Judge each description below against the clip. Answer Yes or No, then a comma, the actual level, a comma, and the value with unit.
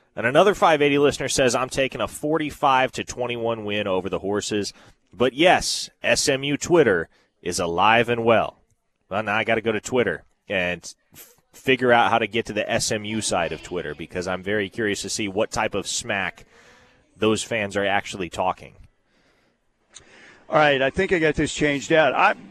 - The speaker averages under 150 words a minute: No, average, 185 wpm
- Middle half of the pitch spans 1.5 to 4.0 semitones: No, average, 5.1 semitones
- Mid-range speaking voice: No, low, 115 Hz